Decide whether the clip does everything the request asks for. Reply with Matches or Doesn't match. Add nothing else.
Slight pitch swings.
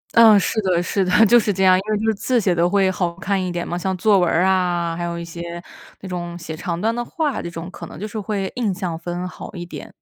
Doesn't match